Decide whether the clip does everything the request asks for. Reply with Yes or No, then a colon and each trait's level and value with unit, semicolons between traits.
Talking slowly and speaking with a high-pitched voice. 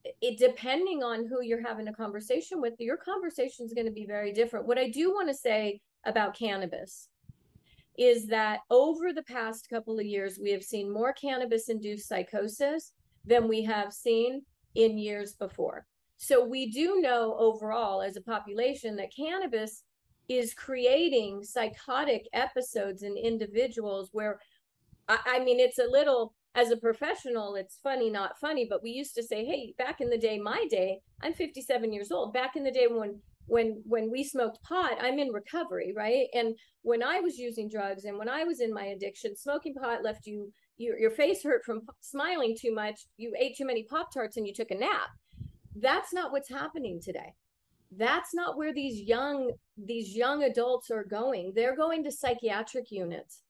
No: average, 185 wpm; high, 235 Hz